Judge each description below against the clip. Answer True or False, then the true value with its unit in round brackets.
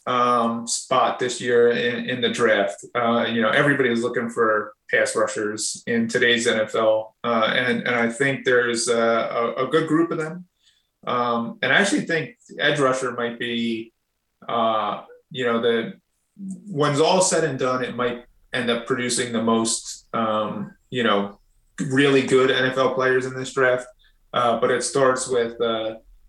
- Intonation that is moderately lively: False (2.3 semitones)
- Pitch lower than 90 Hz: False (120 Hz)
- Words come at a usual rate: True (170 wpm)